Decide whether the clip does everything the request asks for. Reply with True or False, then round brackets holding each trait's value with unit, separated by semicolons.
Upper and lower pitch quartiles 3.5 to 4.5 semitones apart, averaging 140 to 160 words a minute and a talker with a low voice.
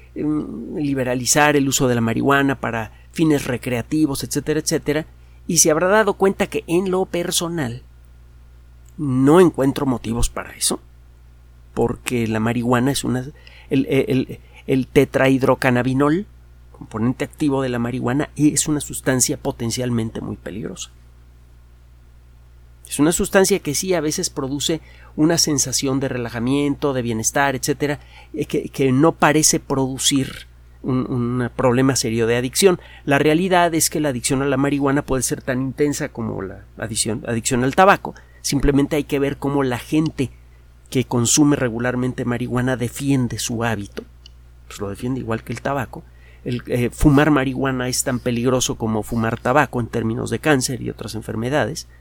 True (4.2 semitones; 150 wpm; 130 Hz)